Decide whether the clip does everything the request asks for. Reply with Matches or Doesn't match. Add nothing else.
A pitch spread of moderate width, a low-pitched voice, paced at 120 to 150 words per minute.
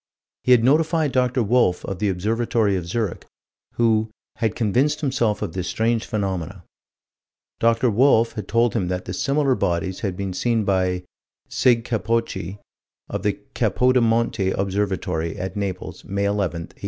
Matches